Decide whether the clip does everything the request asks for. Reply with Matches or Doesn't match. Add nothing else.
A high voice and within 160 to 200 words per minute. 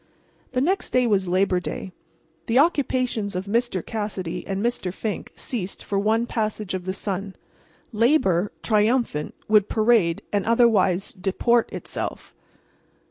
Doesn't match